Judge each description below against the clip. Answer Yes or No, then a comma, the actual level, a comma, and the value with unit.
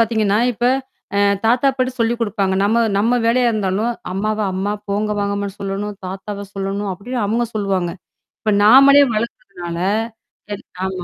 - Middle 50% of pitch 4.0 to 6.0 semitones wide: No, average, 2.8 semitones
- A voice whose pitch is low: No, high, 210 Hz